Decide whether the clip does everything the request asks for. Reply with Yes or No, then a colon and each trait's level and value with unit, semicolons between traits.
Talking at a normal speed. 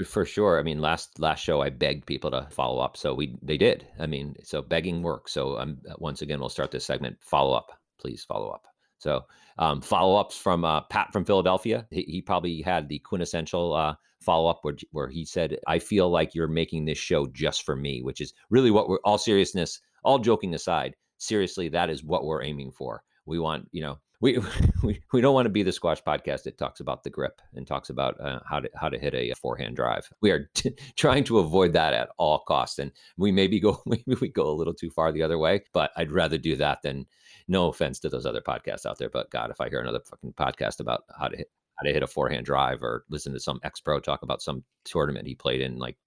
No: fast, 240 wpm